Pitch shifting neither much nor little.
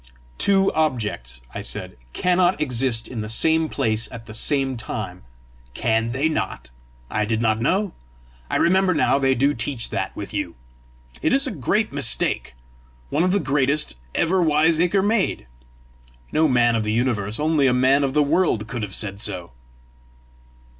No: wide, 6.2 semitones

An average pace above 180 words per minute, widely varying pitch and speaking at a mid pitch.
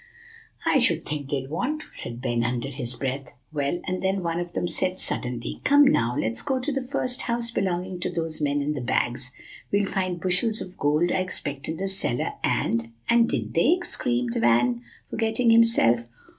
Yes: average, 190 wpm; wide, 8.7 semitones; medium, 165 Hz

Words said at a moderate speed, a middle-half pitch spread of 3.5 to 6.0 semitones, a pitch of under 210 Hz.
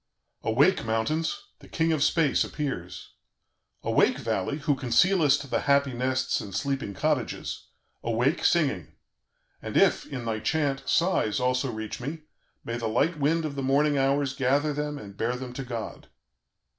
Yes: average, 155 wpm; average, 4.1 semitones; low, 135 Hz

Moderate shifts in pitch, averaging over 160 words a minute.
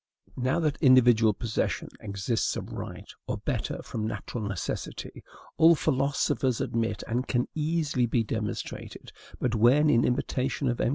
No: average, 3.7 semitones; average, 145 wpm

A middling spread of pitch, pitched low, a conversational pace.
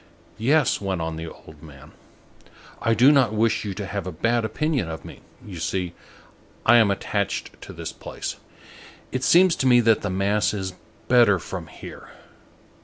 Yes: average, 4.6 semitones; low, 105 Hz; average, 175 wpm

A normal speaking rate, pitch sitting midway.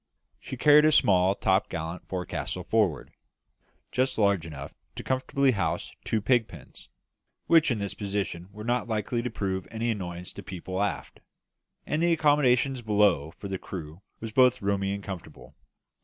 No: average, 155 wpm; low, 100 Hz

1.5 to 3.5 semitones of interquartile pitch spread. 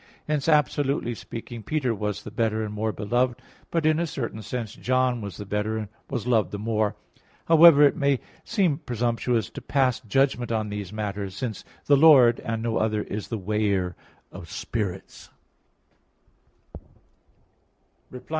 No: average, 4.0 semitones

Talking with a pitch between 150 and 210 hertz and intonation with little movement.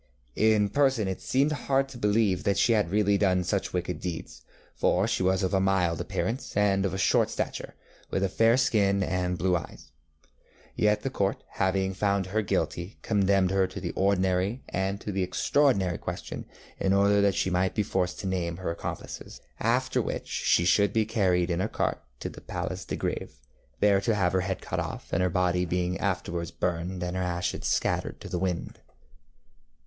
No: very low, 95 Hz; narrow, 2.2 semitones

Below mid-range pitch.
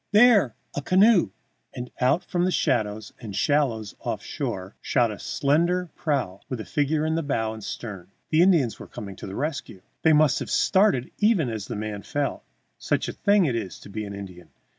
Yes: low, 130 Hz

